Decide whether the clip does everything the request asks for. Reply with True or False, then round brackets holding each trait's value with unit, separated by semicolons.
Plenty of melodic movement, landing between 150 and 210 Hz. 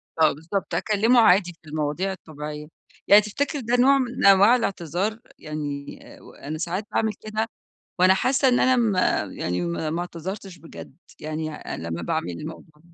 True (6.0 semitones; 185 Hz)